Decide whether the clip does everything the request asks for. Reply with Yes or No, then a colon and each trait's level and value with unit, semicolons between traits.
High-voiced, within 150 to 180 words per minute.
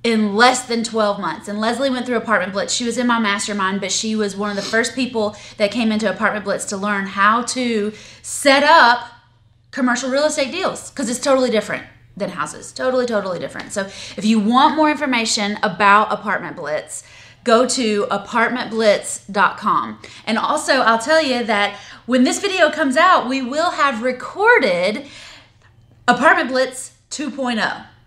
Yes: high, 235 Hz; average, 165 wpm